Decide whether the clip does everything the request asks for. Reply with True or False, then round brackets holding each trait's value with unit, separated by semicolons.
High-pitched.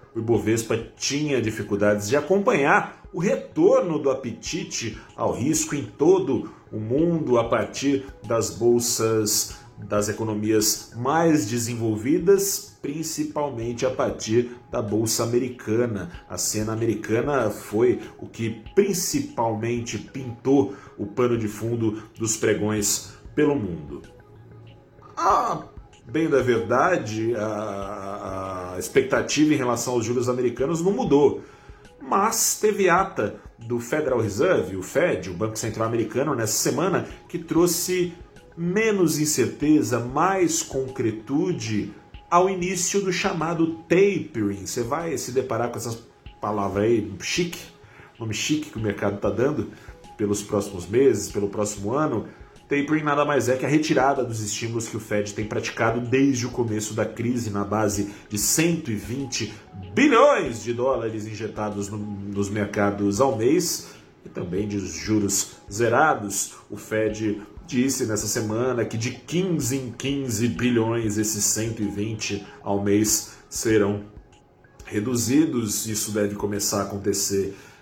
False (115 Hz)